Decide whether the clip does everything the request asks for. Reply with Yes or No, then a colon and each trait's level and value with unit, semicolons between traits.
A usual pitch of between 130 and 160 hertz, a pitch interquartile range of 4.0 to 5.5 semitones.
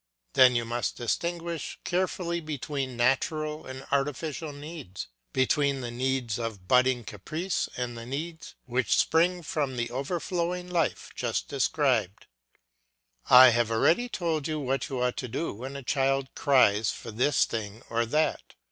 Yes: low, 135 Hz; average, 4.6 semitones